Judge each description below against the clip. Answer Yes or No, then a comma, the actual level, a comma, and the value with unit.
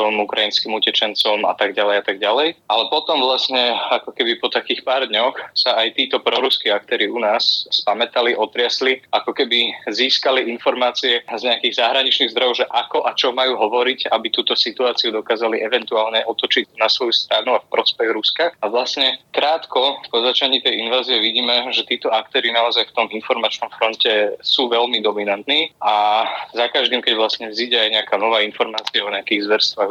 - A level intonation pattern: No, average, 3.1 semitones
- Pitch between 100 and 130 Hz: Yes, low, 120 Hz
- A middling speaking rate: No, fast, 170 wpm